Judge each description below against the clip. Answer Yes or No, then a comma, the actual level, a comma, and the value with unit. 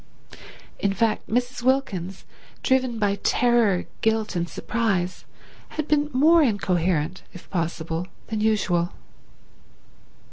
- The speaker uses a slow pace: Yes, slow, 105 wpm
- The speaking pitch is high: Yes, high, 210 Hz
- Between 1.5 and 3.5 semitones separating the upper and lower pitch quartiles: No, average, 5.3 semitones